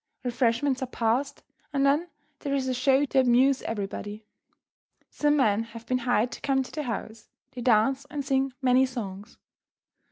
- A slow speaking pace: No, average, 165 wpm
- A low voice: No, very high, 255 Hz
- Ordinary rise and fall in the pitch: Yes, average, 3.0 semitones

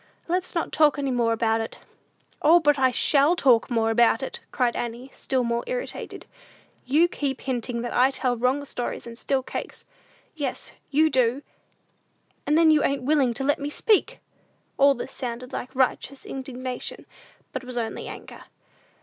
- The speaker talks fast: No, average, 165 wpm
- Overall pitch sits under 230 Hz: No, very high, 260 Hz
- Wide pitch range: No, average, 3.1 semitones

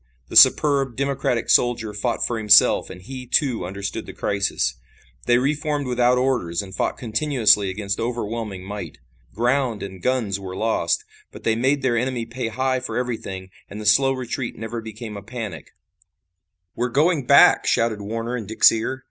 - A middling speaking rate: Yes, average, 170 wpm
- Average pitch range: Yes, average, 3.6 semitones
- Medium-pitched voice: No, low, 115 Hz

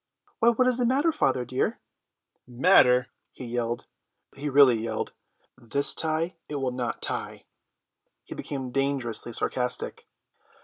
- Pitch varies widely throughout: No, average, 4.3 semitones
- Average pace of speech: No, slow, 130 wpm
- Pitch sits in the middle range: No, low, 130 Hz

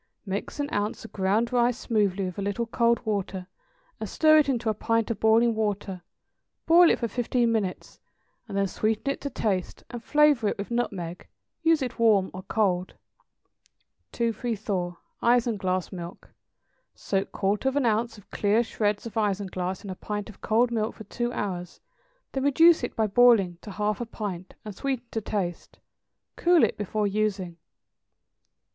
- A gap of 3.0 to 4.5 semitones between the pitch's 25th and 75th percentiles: Yes, average, 3.5 semitones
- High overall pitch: Yes, high, 215 Hz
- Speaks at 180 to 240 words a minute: No, average, 170 wpm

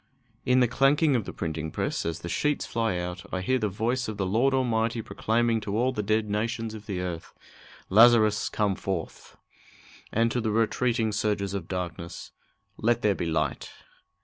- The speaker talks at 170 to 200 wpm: Yes, average, 180 wpm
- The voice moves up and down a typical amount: Yes, average, 3.9 semitones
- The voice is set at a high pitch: No, low, 110 Hz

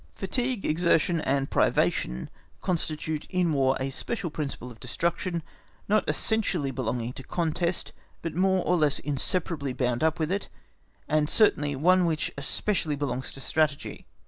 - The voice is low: No, medium, 155 Hz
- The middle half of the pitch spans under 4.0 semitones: No, average, 4.7 semitones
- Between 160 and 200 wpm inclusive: No, average, 145 wpm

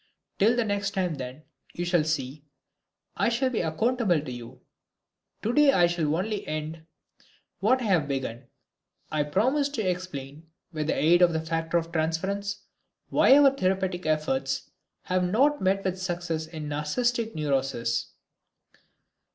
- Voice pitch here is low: No, medium, 175 Hz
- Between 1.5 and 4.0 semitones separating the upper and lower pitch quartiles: No, average, 4.8 semitones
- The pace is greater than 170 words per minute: No, average, 145 wpm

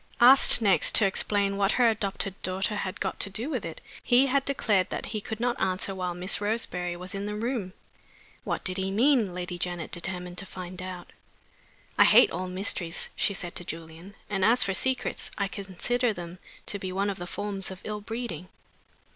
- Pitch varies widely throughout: No, average, 2.9 semitones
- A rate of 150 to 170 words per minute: No, average, 195 wpm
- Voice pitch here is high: Yes, high, 195 Hz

